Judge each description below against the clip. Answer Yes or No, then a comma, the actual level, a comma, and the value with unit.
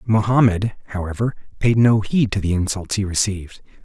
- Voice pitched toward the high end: No, low, 105 Hz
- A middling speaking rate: Yes, average, 155 wpm